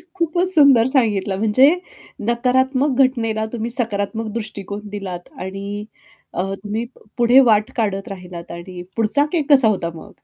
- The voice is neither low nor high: No, high, 220 Hz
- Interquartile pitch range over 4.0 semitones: Yes, average, 4.5 semitones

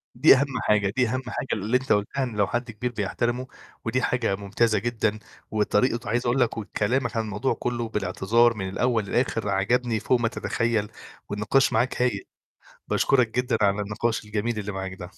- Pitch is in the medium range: No, low, 115 Hz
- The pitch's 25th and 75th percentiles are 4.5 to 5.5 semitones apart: No, average, 3.0 semitones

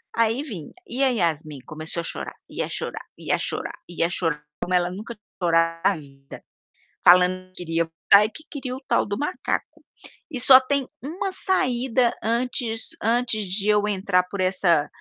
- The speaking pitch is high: Yes, high, 205 Hz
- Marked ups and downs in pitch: Yes, wide, 6.3 semitones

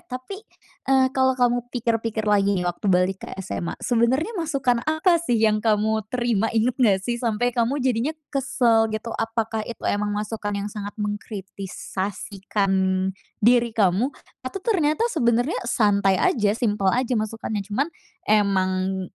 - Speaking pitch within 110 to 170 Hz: No, high, 225 Hz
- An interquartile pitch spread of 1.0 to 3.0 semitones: No, average, 3.4 semitones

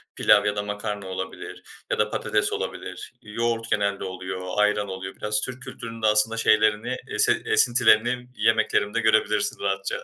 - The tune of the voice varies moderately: No, narrow, 1.9 semitones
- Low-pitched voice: Yes, low, 105 Hz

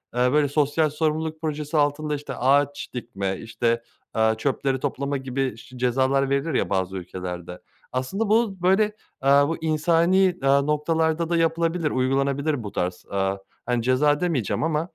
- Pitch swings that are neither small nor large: Yes, average, 4.1 semitones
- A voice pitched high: No, medium, 140 Hz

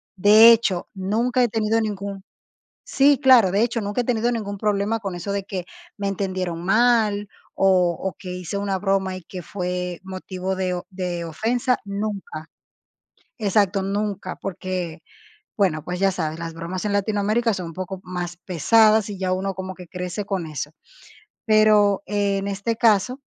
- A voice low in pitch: No, high, 195 Hz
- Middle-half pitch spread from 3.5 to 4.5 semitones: No, average, 2.7 semitones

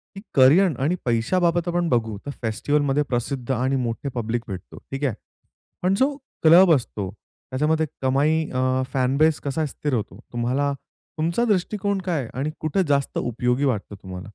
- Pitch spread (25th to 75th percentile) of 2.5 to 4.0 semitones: No, average, 4.7 semitones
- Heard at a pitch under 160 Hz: Yes, medium, 140 Hz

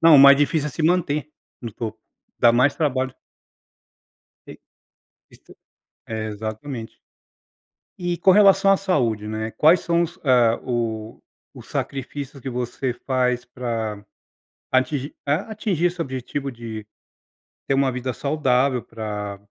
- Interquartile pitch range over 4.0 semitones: Yes, average, 4.7 semitones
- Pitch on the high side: No, low, 130 Hz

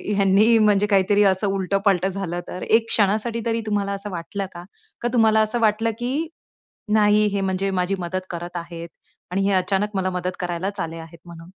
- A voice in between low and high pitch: No, high, 195 Hz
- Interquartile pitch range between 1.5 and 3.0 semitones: Yes, average, 2.7 semitones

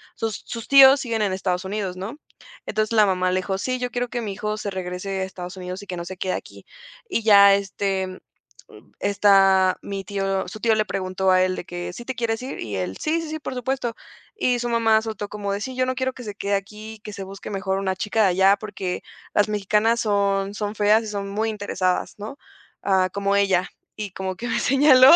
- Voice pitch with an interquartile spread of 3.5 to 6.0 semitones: No, average, 2.8 semitones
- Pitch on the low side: No, high, 200 Hz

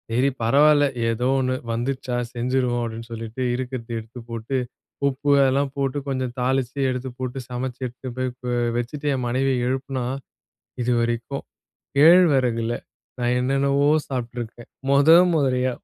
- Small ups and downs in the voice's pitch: Yes, narrow, 2.1 semitones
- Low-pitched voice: Yes, low, 125 Hz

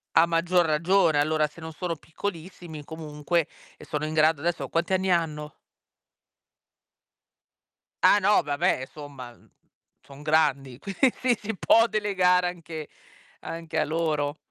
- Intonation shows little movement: No, average, 3.1 semitones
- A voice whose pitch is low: No, medium, 160 Hz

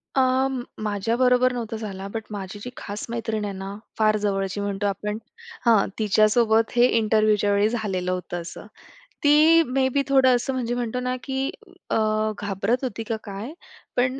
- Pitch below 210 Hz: No, high, 220 Hz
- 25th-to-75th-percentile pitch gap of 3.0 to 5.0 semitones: Yes, average, 3.6 semitones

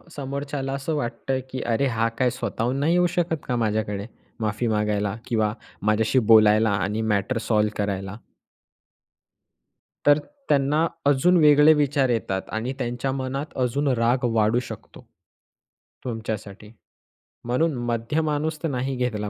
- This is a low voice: Yes, low, 125 Hz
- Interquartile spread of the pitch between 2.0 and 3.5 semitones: No, average, 4.5 semitones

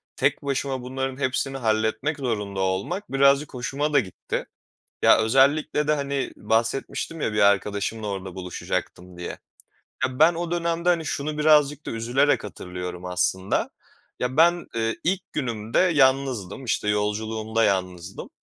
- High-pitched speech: No, low, 125 Hz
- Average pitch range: No, wide, 5.9 semitones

